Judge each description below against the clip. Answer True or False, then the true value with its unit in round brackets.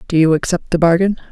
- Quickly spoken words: True (230 wpm)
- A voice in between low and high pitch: True (170 Hz)